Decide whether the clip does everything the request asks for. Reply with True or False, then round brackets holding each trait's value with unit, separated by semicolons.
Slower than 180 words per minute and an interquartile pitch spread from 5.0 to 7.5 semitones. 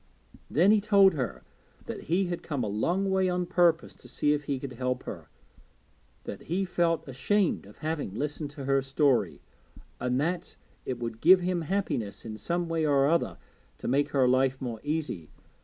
False (185 wpm; 5.3 semitones)